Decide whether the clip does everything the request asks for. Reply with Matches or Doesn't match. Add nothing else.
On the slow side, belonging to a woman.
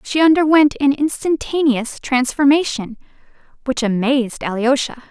Matches